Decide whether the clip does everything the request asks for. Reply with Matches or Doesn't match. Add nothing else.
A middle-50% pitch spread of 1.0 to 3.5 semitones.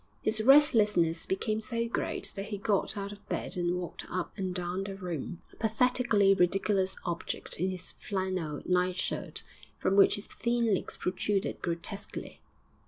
Matches